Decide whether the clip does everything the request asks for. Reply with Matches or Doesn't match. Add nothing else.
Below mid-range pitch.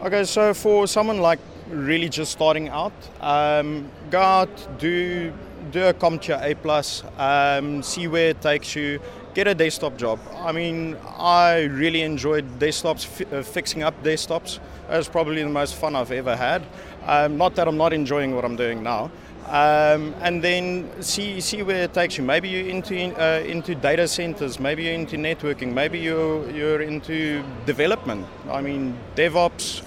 Doesn't match